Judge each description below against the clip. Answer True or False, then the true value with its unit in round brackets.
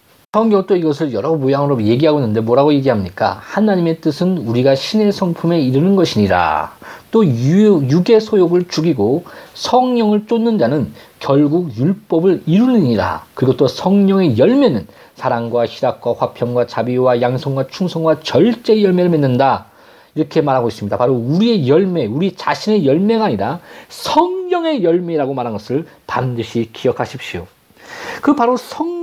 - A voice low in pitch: False (165 Hz)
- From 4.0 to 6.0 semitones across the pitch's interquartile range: False (7.8 semitones)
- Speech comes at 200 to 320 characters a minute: False (335 characters per minute)